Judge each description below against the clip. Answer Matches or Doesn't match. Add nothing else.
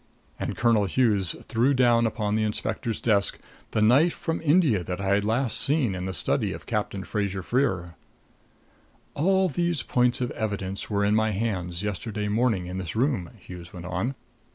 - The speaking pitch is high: Doesn't match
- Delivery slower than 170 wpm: Doesn't match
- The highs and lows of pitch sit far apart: Doesn't match